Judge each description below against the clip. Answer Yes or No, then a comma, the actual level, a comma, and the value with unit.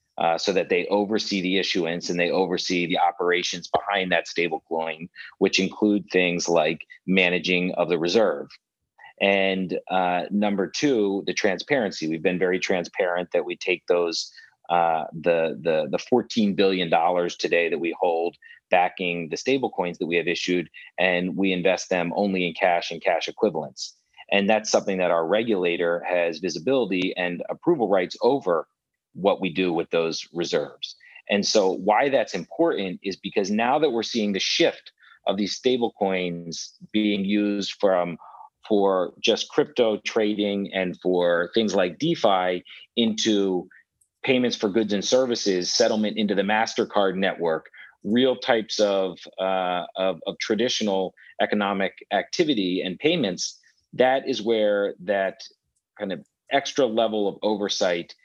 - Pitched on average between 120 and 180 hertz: No, very low, 95 Hz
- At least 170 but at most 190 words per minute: No, average, 150 wpm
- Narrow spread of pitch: No, average, 3.0 semitones